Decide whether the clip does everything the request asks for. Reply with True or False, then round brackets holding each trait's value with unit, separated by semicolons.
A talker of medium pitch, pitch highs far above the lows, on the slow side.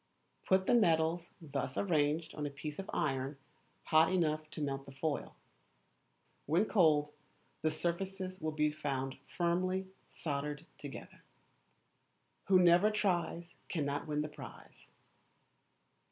False (160 Hz; 3.2 semitones; 125 wpm)